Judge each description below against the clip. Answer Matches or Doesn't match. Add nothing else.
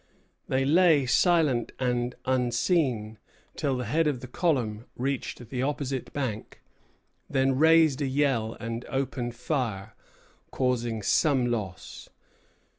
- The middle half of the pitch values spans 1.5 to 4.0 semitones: Matches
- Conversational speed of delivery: Doesn't match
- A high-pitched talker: Doesn't match